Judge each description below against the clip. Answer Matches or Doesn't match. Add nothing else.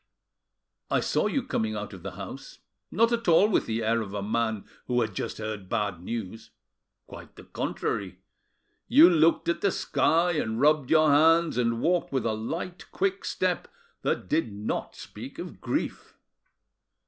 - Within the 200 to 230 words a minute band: Doesn't match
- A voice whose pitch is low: Matches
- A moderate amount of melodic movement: Doesn't match